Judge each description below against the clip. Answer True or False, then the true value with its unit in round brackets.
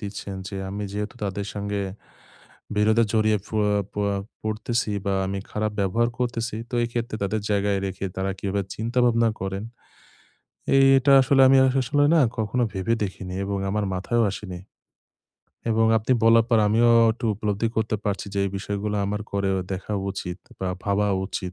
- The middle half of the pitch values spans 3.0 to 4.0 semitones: False (2.6 semitones)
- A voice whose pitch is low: True (105 Hz)